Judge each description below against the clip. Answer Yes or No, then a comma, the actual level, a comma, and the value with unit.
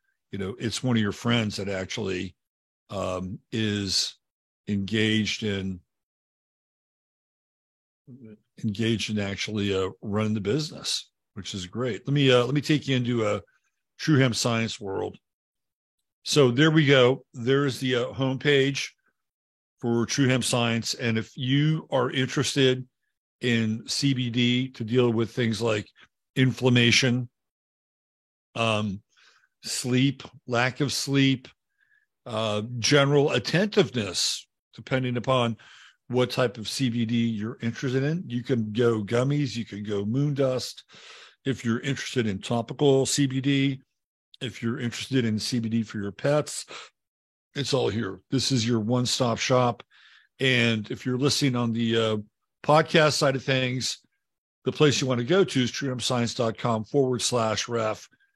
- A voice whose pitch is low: Yes, low, 125 Hz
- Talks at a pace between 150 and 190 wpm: No, slow, 135 wpm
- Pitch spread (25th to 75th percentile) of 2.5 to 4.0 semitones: Yes, average, 3.2 semitones